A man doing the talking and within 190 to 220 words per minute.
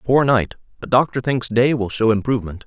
Yes: male; fast, 205 wpm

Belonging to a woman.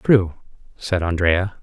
No: male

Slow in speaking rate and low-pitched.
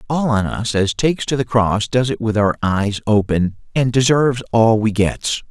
No: fast, 205 wpm; low, 115 Hz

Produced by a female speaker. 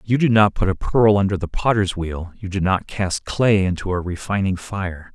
No: male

